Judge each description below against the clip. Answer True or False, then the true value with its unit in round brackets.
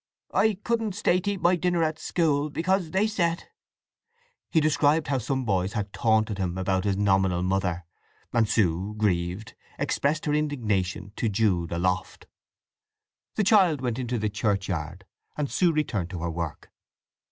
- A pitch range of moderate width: False (8.8 semitones)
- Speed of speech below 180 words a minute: True (155 wpm)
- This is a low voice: True (110 Hz)